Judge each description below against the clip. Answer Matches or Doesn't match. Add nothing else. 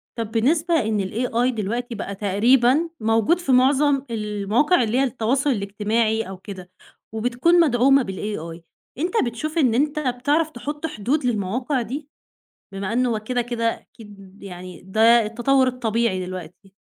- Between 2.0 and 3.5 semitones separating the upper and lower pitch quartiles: Doesn't match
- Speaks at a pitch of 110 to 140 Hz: Doesn't match